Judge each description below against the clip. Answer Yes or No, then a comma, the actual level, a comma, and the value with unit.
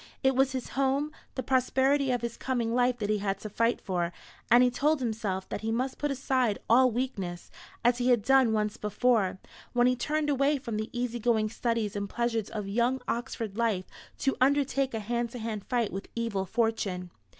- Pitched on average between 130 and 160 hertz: No, high, 235 Hz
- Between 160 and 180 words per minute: No, average, 200 wpm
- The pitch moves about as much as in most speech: Yes, average, 3.4 semitones